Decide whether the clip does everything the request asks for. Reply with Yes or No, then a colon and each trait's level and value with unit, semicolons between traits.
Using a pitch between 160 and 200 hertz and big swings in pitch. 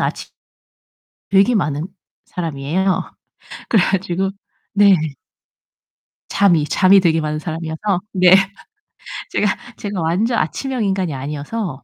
No: medium, 185 Hz; average, 3.9 semitones